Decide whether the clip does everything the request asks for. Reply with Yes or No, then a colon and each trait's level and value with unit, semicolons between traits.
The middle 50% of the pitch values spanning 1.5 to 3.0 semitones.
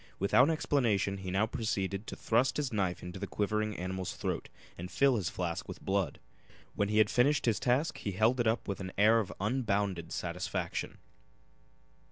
No: average, 3.8 semitones